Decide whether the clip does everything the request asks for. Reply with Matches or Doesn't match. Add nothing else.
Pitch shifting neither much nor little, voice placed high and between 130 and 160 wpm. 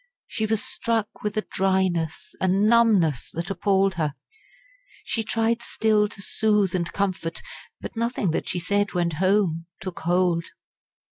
Matches